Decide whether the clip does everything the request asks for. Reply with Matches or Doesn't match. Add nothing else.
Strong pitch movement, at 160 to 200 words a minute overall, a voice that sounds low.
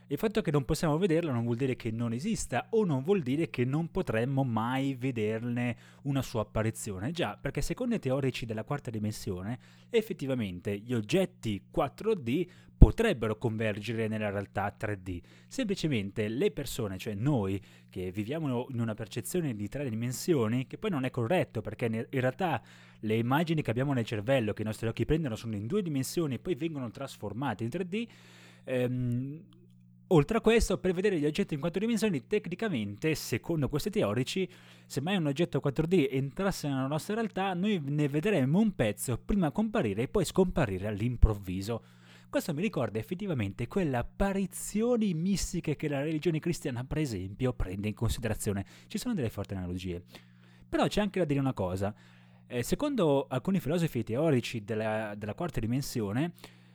Matches